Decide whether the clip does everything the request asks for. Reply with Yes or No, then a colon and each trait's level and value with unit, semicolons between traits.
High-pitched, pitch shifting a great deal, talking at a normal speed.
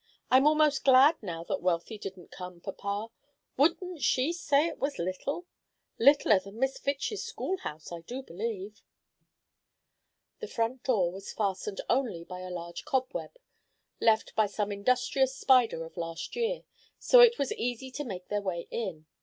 Yes: high, 225 Hz; wide, 6.9 semitones; average, 155 wpm